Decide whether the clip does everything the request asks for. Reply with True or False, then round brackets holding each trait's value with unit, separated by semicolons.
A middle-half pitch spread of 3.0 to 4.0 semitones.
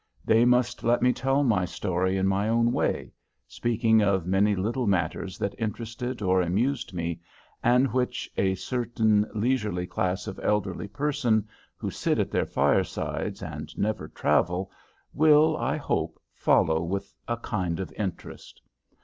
False (4.5 semitones)